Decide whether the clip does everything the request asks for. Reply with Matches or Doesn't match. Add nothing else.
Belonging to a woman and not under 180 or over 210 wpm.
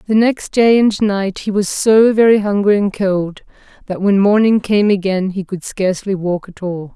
Matches